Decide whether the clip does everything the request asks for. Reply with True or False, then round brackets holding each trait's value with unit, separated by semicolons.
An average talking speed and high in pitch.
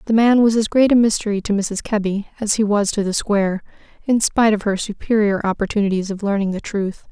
False (220 wpm; 210 Hz)